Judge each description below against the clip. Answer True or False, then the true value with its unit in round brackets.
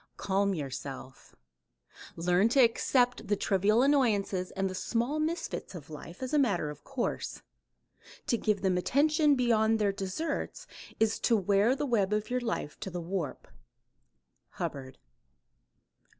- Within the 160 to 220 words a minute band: False (140 wpm)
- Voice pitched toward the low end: False (210 Hz)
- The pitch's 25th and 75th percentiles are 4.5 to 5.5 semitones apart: True (5.2 semitones)